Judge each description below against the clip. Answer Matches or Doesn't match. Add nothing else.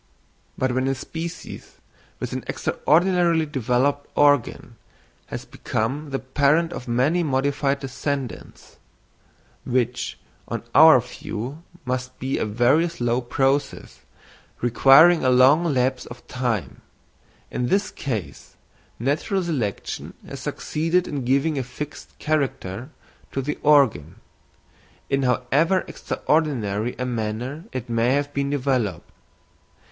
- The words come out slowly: Matches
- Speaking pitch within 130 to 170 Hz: Matches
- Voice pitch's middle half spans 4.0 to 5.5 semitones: Doesn't match